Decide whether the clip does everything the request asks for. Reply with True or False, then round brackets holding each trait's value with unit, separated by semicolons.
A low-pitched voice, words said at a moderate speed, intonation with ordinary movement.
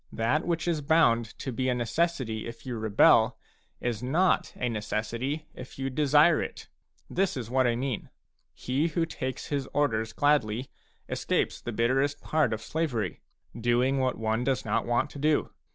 True (130 Hz; 170 wpm; 4.1 semitones)